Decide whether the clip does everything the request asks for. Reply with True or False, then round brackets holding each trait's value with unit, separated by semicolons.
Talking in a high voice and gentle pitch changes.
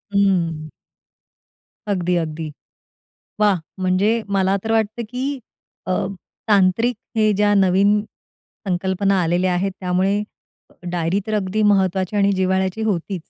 True (195 Hz; 2.3 semitones)